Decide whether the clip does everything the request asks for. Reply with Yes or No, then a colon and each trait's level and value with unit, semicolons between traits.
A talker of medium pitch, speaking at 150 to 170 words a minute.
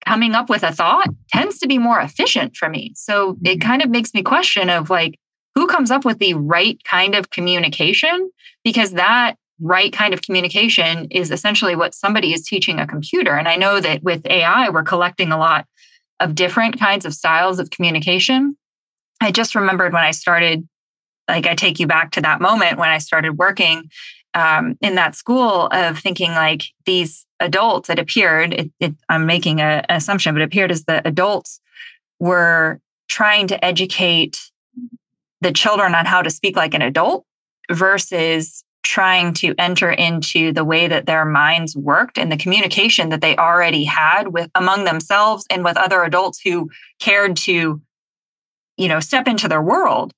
No: medium, 180 Hz; average, 180 wpm